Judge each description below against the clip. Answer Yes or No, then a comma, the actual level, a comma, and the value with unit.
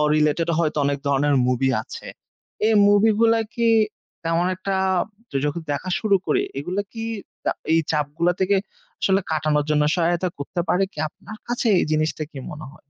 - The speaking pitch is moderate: Yes, medium, 165 Hz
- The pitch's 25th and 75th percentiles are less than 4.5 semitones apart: No, average, 4.8 semitones